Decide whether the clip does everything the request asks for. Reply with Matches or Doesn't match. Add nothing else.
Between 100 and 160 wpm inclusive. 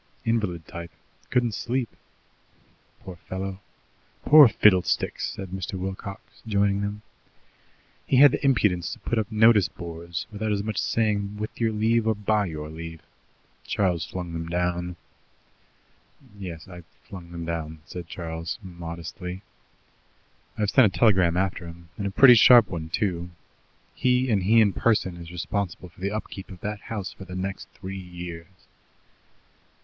Matches